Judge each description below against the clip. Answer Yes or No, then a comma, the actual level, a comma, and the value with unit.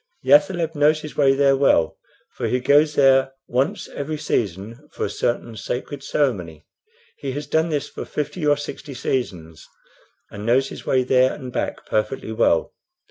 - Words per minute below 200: Yes, average, 170 wpm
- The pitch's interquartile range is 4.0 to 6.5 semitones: No, average, 3.6 semitones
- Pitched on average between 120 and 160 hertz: Yes, low, 135 Hz